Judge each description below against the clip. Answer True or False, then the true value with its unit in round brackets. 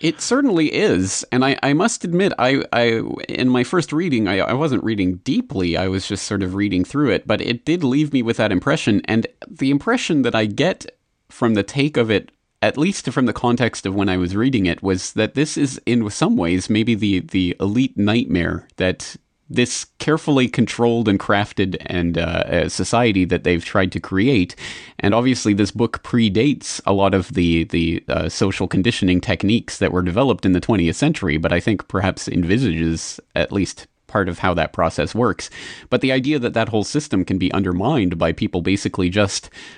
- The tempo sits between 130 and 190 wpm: False (200 wpm)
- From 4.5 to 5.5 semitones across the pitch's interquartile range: True (5.2 semitones)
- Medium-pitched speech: False (105 Hz)